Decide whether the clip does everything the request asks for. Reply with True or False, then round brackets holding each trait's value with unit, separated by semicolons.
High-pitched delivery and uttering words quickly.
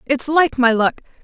False (265 Hz; 195 wpm)